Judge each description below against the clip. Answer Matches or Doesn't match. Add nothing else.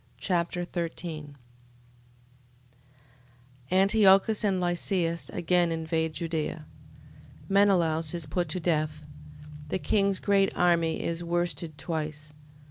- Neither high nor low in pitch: Matches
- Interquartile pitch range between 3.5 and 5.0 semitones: Doesn't match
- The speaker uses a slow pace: Matches